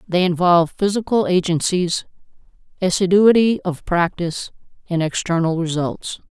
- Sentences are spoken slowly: Yes, slow, 95 wpm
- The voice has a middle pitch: Yes, medium, 180 Hz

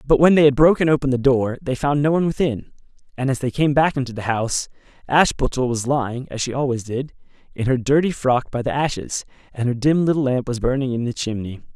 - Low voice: Yes, low, 130 Hz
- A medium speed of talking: No, fast, 230 wpm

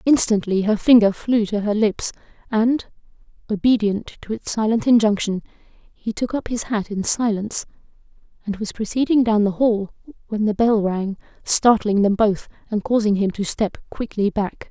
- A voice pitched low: No, high, 215 Hz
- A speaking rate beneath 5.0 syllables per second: Yes, 4.7 syllables/s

